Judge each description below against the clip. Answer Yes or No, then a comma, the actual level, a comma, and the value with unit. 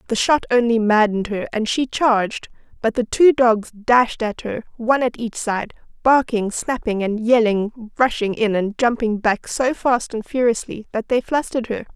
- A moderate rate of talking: Yes, average, 180 wpm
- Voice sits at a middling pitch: No, high, 230 Hz